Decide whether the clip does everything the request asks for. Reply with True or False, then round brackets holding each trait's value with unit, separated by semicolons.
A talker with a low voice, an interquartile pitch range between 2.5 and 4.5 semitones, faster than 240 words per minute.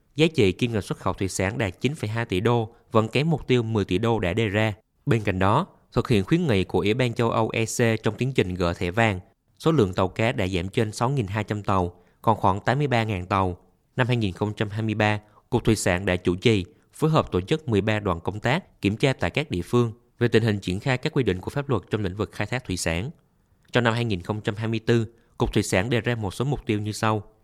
False (110 Hz; 3.6 semitones; 235 wpm)